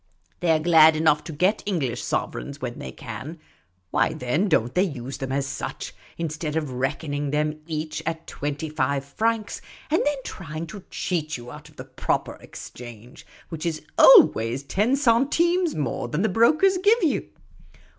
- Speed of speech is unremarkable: Yes, average, 165 wpm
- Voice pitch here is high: No, medium, 155 Hz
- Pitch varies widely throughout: Yes, wide, 6.3 semitones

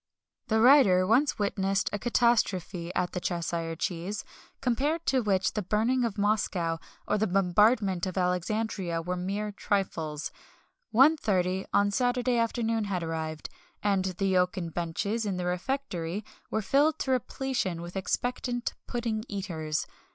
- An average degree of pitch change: Yes, average, 4.4 semitones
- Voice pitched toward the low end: No, high, 200 Hz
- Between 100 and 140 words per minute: Yes, slow, 135 wpm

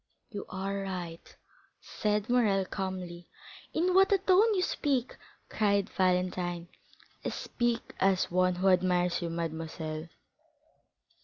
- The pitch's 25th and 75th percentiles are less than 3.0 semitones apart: No, average, 4.0 semitones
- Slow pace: Yes, slow, 120 wpm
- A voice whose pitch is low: No, high, 190 Hz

